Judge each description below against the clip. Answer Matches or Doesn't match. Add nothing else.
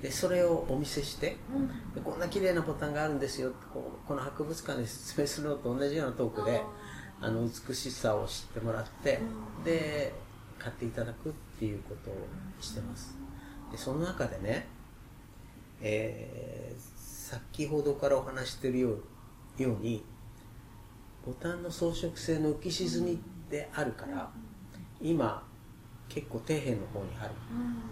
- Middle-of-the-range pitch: Doesn't match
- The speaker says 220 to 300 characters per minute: Matches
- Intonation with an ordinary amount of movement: Matches